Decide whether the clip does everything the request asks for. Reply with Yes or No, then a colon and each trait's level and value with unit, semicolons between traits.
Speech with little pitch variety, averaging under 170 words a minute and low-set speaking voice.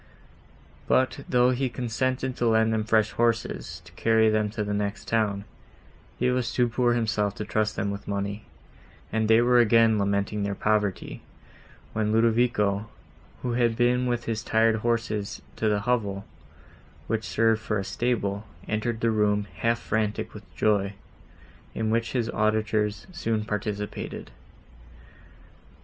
Yes: narrow, 2.0 semitones; average, 145 wpm; low, 110 Hz